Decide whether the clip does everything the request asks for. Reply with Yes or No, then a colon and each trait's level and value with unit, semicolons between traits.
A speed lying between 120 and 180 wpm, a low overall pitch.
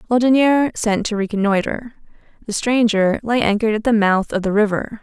No: average, 165 wpm; high, 220 Hz